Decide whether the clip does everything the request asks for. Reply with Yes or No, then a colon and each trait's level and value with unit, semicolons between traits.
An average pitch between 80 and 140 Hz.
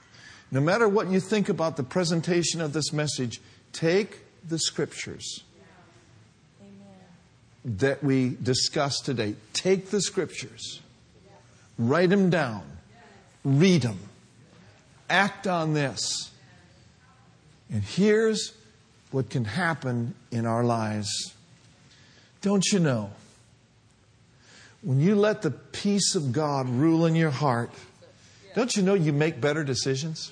Yes: low, 135 Hz